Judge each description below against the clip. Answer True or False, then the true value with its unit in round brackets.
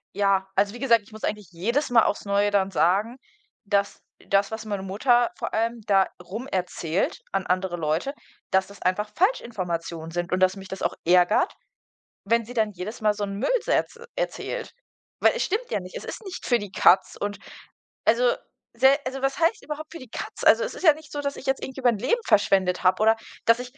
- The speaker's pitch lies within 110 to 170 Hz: False (210 Hz)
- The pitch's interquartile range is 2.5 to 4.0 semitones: False (5.2 semitones)